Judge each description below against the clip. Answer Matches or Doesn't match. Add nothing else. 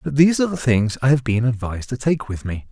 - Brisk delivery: Matches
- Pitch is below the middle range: Matches